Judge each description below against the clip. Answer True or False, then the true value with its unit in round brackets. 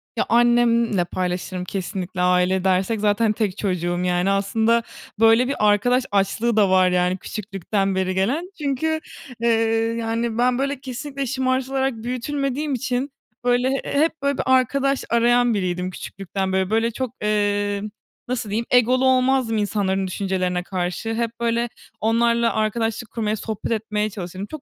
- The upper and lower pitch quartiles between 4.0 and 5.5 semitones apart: True (4.4 semitones)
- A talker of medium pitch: False (225 Hz)